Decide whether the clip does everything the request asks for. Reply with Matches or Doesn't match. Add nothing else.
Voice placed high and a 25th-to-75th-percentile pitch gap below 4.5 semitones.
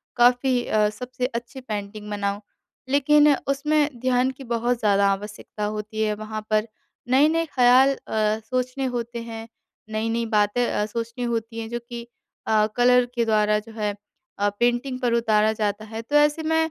Matches